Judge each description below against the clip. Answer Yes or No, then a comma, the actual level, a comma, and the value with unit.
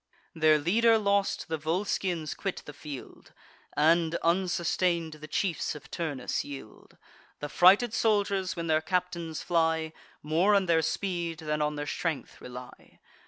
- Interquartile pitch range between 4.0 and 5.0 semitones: No, average, 3.2 semitones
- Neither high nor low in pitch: Yes, medium, 165 Hz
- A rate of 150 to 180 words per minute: No, average, 140 wpm